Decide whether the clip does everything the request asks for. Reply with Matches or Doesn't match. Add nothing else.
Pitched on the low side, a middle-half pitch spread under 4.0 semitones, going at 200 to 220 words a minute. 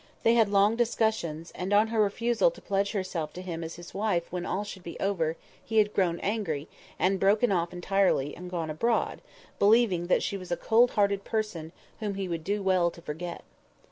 Doesn't match